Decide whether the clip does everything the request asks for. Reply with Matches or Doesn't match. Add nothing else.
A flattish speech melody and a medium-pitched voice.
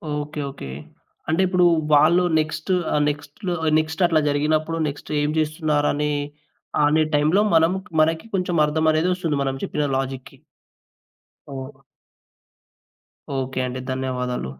Matches